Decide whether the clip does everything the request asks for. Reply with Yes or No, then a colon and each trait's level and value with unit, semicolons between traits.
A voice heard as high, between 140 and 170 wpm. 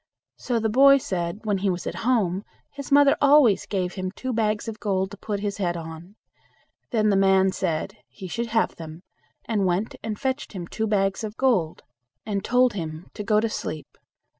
No: high, 205 Hz; average, 195 wpm